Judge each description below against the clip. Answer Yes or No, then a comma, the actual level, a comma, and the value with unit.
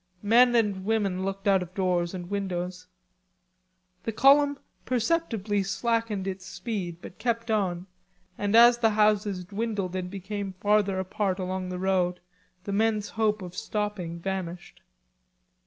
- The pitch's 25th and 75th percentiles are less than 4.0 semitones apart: Yes, average, 2.9 semitones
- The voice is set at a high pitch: Yes, high, 200 Hz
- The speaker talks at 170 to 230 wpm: No, average, 140 wpm